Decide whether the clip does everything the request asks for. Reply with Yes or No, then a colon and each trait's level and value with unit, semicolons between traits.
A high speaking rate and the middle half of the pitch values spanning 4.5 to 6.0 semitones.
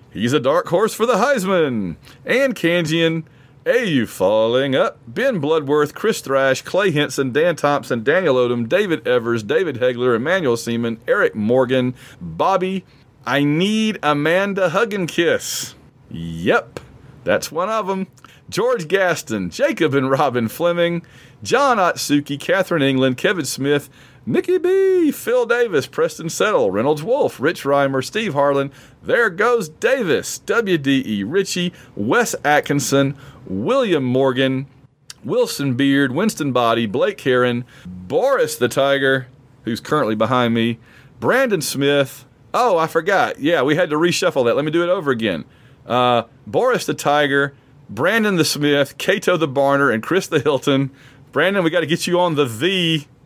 No: average, 145 wpm; wide, 5.5 semitones